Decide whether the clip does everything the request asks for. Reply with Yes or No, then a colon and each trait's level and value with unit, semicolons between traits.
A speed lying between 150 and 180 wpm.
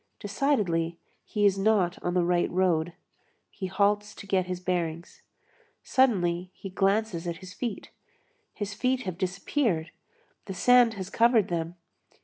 No: average, 140 wpm